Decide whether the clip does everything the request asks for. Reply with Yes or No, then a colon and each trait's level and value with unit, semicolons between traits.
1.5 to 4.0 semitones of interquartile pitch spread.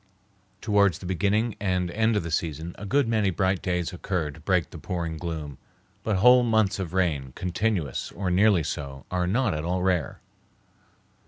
Yes: average, 3.7 semitones